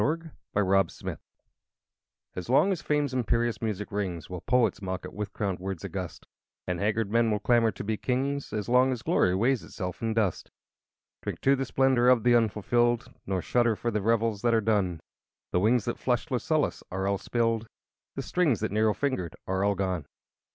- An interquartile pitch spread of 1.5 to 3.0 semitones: No, average, 3.8 semitones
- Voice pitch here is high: No, low, 110 Hz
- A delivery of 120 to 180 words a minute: No, average, 195 wpm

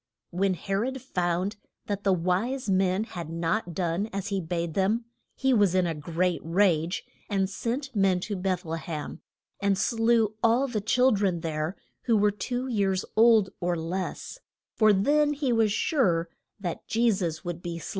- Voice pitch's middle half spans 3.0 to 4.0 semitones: No, average, 4.4 semitones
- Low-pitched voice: No, high, 195 Hz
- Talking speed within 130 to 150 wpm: No, average, 175 wpm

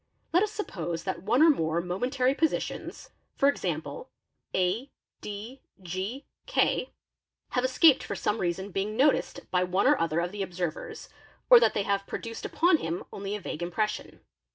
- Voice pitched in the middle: No, high, 205 Hz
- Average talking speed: Yes, average, 165 wpm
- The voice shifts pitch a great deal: Yes, wide, 7.0 semitones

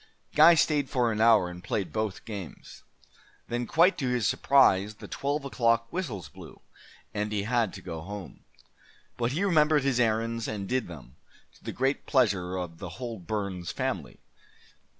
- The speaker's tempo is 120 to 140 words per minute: No, average, 170 wpm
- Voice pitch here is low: Yes, low, 115 Hz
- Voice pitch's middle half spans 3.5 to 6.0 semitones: Yes, average, 5.2 semitones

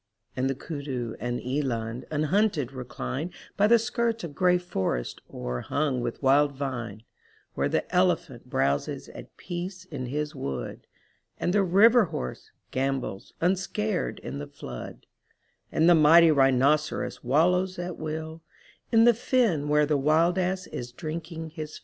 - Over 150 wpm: No, average, 145 wpm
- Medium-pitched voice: Yes, medium, 155 Hz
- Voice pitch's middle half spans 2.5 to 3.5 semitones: No, average, 5.3 semitones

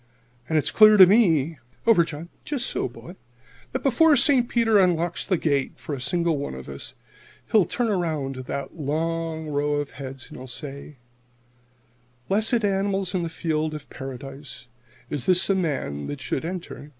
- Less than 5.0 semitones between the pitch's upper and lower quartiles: No, wide, 5.4 semitones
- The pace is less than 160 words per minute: No, average, 175 wpm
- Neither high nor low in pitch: Yes, medium, 165 Hz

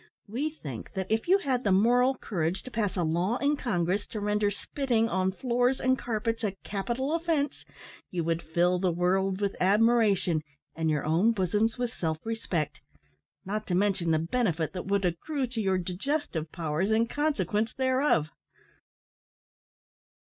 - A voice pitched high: Yes, high, 205 Hz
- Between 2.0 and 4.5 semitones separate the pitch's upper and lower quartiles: No, wide, 5.5 semitones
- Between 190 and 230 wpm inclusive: No, average, 160 wpm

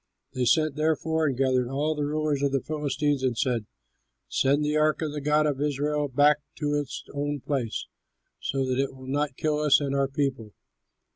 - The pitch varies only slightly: Yes, narrow, 2.0 semitones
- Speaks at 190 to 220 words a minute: Yes, average, 195 wpm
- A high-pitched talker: No, medium, 145 Hz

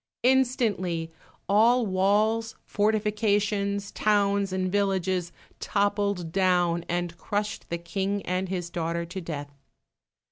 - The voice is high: Yes, high, 195 Hz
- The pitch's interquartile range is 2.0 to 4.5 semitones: Yes, average, 2.9 semitones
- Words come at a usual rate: No, slow, 105 wpm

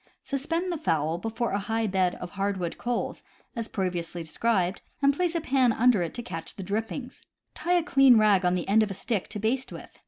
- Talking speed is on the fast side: Yes, fast, 210 wpm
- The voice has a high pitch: Yes, high, 220 Hz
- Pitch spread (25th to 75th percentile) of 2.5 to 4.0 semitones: No, wide, 5.5 semitones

